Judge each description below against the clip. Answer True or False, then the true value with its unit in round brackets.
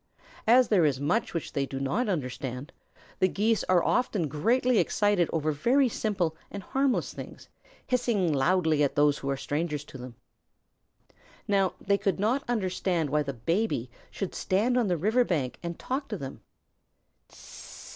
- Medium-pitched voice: True (180 Hz)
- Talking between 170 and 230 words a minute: False (160 wpm)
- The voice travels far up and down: True (7.0 semitones)